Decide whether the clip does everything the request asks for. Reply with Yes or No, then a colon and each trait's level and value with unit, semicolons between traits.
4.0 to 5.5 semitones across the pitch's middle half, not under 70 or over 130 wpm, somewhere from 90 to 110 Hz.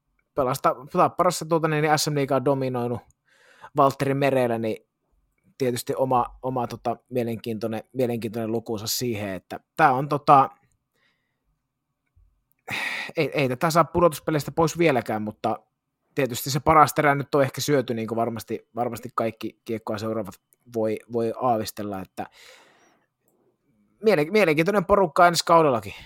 No: average, 4.4 semitones; average, 120 wpm; low, 125 Hz